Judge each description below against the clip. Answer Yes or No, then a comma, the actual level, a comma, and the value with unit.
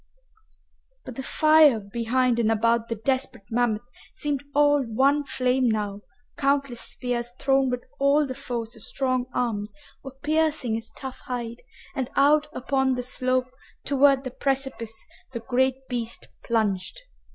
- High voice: Yes, very high, 255 Hz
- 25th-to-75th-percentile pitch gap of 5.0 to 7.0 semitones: No, average, 2.8 semitones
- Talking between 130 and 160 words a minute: Yes, average, 140 wpm